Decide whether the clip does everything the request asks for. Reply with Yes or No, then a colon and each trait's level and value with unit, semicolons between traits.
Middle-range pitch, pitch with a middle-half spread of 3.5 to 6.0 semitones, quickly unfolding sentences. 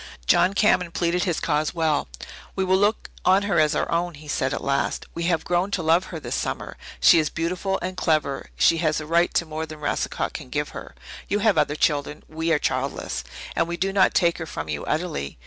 No: medium, 165 Hz; average, 2.9 semitones; fast, 225 wpm